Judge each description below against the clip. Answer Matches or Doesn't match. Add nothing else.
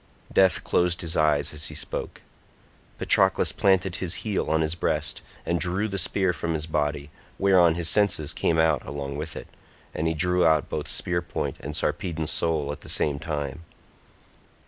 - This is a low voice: Matches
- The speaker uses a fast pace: Doesn't match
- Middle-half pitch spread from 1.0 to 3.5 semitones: Matches